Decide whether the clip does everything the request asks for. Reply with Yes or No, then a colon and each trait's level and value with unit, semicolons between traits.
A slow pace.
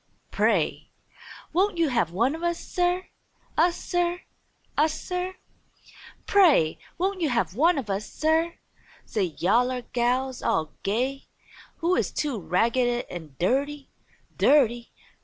Yes: slow, 125 wpm